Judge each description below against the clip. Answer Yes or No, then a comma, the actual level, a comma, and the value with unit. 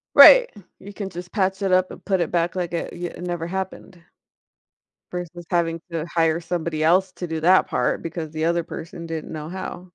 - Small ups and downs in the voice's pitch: Yes, narrow, 2.0 semitones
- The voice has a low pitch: No, medium, 175 Hz